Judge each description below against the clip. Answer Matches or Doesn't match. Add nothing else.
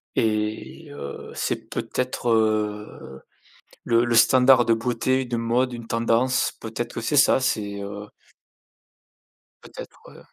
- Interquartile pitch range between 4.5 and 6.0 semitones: Doesn't match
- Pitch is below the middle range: Matches